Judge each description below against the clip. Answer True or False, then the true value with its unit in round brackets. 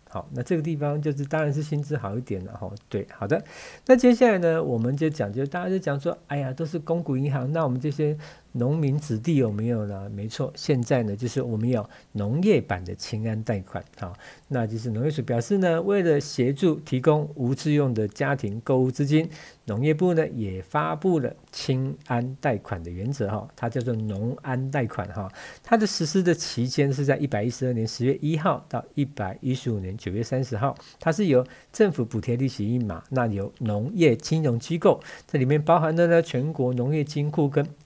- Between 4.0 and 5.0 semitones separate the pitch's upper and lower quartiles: True (4.7 semitones)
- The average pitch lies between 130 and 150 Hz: True (135 Hz)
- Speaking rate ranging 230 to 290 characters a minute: False (300 characters per minute)